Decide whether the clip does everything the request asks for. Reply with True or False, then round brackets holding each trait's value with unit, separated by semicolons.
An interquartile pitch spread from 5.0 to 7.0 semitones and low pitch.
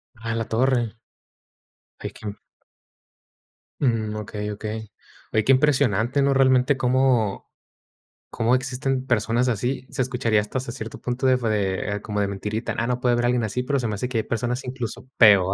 False (2.8 semitones; 120 Hz)